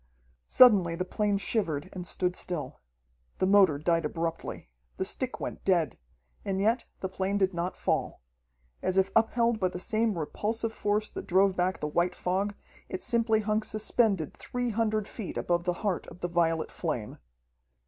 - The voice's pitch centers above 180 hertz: Yes, high, 190 Hz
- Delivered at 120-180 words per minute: Yes, average, 170 wpm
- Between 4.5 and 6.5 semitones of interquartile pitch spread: No, average, 3.7 semitones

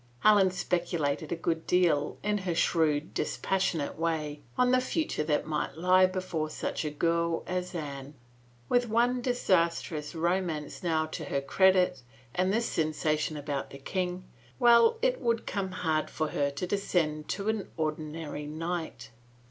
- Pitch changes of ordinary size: Yes, average, 3.7 semitones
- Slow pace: No, average, 155 wpm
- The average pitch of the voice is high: No, medium, 170 Hz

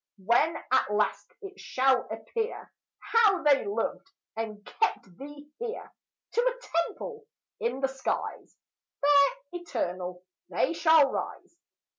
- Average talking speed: No, slow, 120 wpm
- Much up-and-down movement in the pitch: Yes, wide, 7.6 semitones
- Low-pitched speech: No, very high, 290 Hz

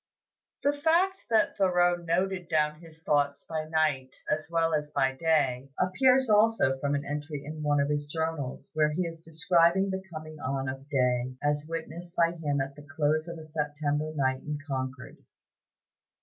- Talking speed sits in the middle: Yes, average, 175 wpm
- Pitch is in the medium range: Yes, medium, 155 Hz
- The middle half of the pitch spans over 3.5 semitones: No, average, 2.8 semitones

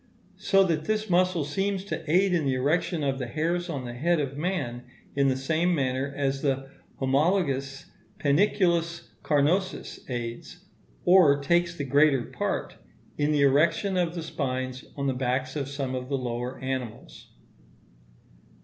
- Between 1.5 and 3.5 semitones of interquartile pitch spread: No, average, 4.6 semitones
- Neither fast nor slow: Yes, average, 155 wpm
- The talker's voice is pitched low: No, medium, 145 Hz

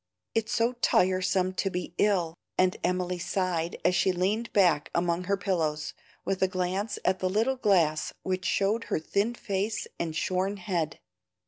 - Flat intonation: Yes, narrow, 2.1 semitones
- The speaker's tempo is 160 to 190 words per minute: Yes, average, 165 wpm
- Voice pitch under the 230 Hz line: Yes, medium, 185 Hz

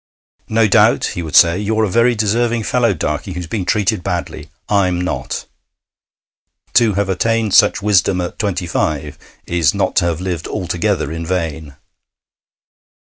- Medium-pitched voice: No, very low, 95 Hz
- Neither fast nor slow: Yes, average, 150 wpm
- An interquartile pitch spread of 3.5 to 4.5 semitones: Yes, average, 3.9 semitones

